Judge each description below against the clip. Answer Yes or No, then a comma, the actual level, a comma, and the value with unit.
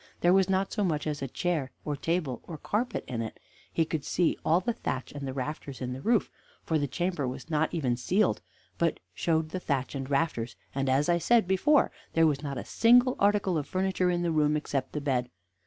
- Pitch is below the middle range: No, medium, 155 Hz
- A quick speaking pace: Yes, fast, 220 wpm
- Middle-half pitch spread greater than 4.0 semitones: Yes, average, 5.0 semitones